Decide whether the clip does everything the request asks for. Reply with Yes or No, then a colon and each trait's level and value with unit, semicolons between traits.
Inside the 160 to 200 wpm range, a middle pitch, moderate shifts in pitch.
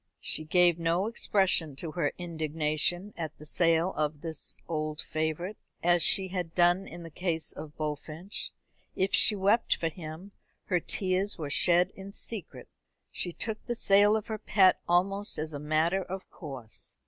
Yes: average, 165 wpm; medium, 175 Hz; average, 3.5 semitones